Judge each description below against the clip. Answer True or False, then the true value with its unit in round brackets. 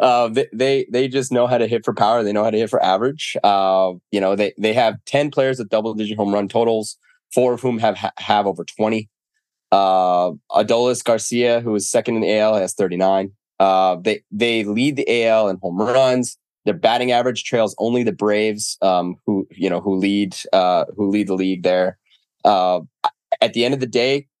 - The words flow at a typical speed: False (210 wpm)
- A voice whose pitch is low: True (110 Hz)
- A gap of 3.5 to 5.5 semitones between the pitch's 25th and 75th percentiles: True (3.8 semitones)